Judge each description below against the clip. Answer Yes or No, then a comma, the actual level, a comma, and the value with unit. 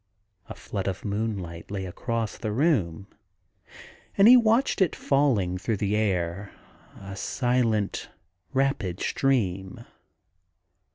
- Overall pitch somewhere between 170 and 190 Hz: No, low, 105 Hz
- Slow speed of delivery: Yes, slow, 110 wpm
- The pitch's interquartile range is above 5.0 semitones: Yes, wide, 5.6 semitones